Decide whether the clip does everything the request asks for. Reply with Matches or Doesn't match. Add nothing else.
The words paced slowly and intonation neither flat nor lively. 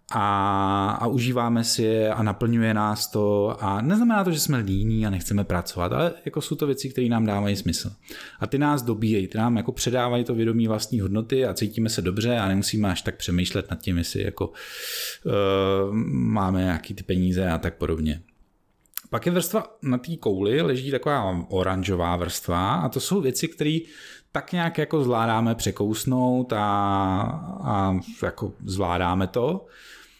Doesn't match